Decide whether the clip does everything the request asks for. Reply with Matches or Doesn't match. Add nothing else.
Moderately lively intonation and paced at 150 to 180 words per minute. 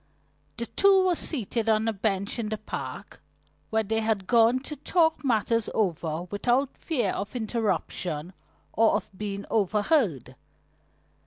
Doesn't match